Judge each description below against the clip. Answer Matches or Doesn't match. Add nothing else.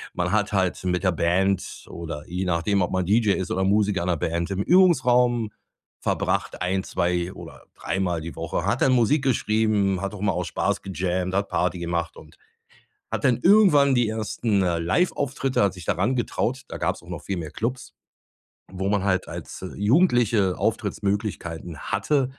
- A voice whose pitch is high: Doesn't match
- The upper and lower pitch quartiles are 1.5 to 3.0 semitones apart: Doesn't match